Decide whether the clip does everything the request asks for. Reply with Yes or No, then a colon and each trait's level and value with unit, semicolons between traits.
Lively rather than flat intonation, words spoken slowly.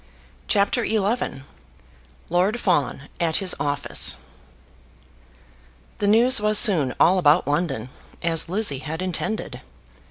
Yes: wide, 5.9 semitones; slow, 105 wpm